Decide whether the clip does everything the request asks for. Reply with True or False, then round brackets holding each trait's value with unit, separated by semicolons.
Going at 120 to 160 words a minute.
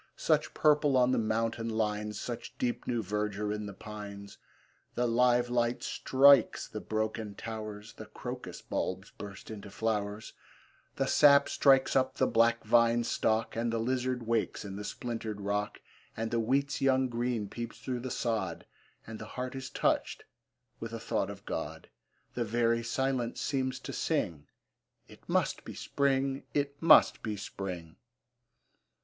True (155 wpm)